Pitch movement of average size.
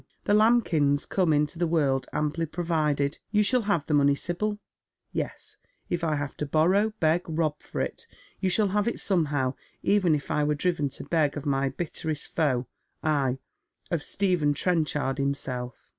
Yes: average, 3.8 semitones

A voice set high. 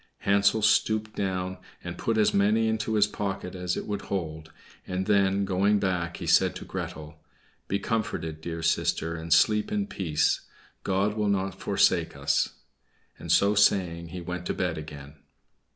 No: very low, 95 Hz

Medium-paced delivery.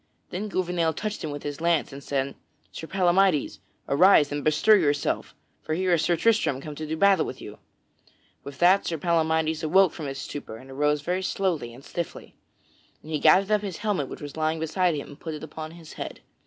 No: fast, 210 wpm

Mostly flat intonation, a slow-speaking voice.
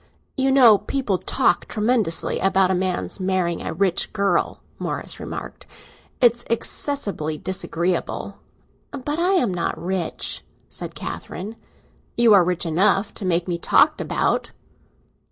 No: average, 4.6 semitones; slow, 130 wpm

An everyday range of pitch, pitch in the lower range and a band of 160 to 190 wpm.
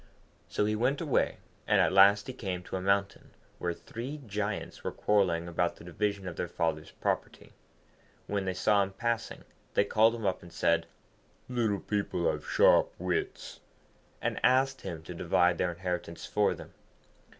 Yes: average, 4.4 semitones; low, 100 Hz; average, 170 wpm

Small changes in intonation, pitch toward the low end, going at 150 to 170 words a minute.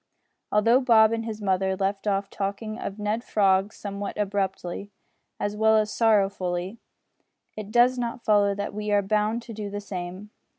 No: narrow, 1.9 semitones; high, 205 Hz; average, 165 wpm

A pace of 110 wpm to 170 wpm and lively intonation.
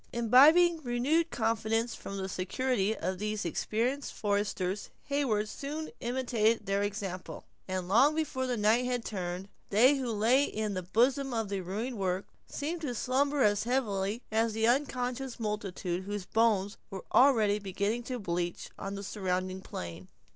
No: average, 155 wpm; average, 4.3 semitones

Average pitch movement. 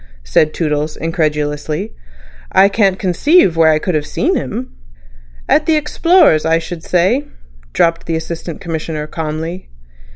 Yes: average, 4.1 semitones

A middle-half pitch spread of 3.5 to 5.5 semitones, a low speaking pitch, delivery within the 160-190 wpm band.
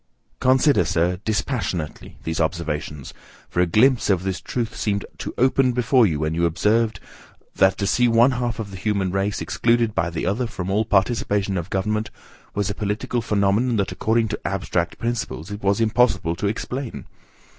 Yes: average, 3.9 semitones; low, 105 Hz; average, 175 wpm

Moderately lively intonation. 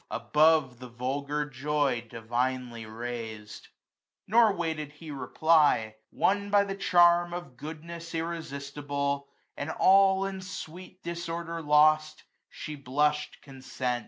Yes: average, 4.6 semitones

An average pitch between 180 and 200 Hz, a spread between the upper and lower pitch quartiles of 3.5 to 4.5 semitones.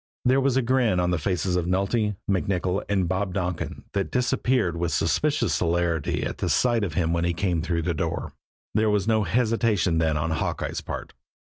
No: very low, 95 Hz; average, 4.2 semitones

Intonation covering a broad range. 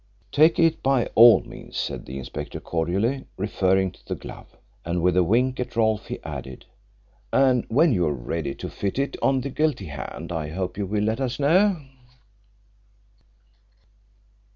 Yes: wide, 7.2 semitones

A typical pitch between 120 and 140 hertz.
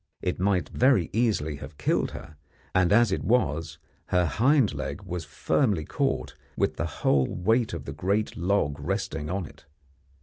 No: very low, 90 Hz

